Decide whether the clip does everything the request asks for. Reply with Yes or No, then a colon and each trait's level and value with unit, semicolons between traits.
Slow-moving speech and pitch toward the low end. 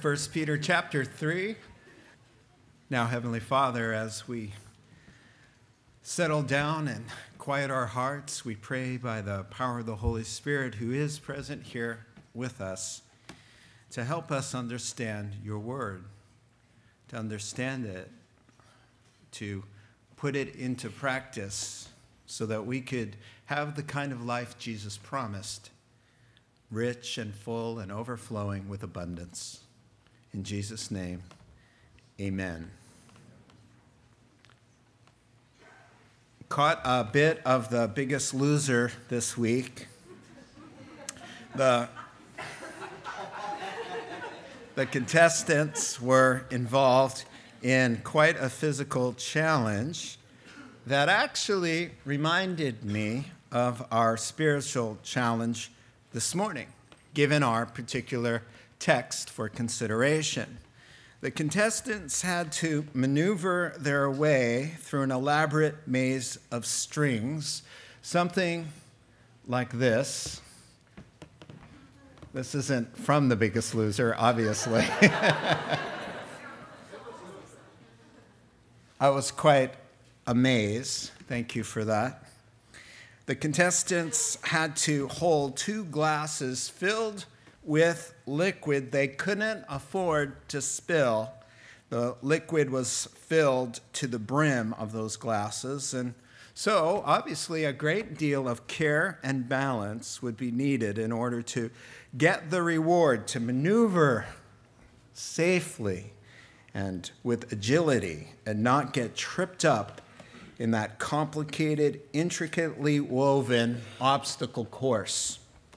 Yes: slow, 100 wpm; low, 125 Hz